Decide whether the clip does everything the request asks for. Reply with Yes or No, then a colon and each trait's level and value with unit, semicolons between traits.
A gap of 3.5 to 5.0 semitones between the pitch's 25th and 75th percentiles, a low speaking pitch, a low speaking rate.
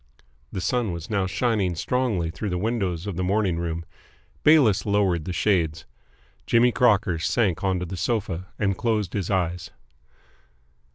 No: average, 3.8 semitones; very low, 95 Hz; average, 150 wpm